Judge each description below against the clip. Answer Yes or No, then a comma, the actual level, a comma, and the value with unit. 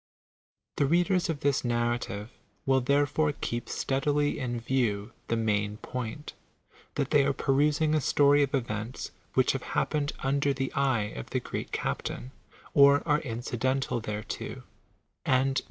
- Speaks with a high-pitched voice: No, low, 135 Hz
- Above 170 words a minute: No, average, 155 wpm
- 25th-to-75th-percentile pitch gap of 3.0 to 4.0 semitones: Yes, average, 3.5 semitones